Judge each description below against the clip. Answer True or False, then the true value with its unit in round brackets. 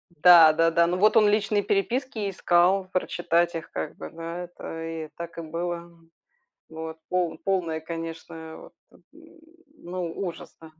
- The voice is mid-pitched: True (170 Hz)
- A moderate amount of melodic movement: False (2.1 semitones)